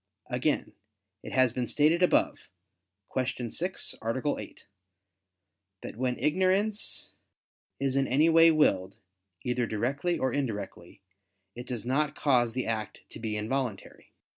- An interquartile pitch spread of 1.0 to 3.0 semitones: No, average, 4.6 semitones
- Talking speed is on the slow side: Yes, slow, 130 wpm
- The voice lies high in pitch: No, low, 130 Hz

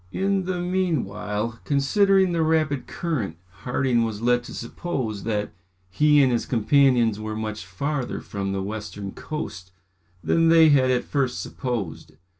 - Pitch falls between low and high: No, low, 125 Hz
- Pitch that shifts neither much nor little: No, wide, 6.4 semitones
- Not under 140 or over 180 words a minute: Yes, average, 145 wpm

